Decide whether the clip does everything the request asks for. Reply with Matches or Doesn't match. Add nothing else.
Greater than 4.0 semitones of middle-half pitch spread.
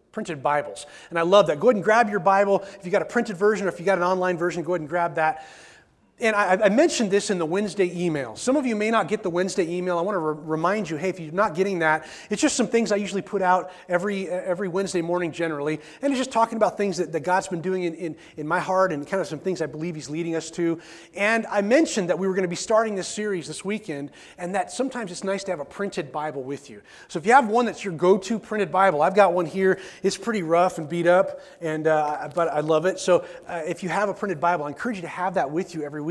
Doesn't match